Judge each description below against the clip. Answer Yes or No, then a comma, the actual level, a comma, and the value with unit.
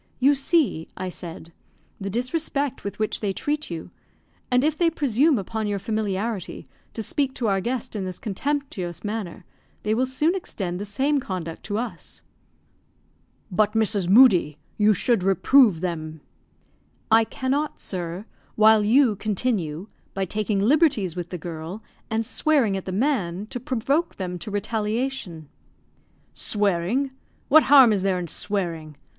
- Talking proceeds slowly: No, average, 150 wpm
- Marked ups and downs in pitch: Yes, wide, 5.9 semitones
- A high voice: Yes, high, 210 Hz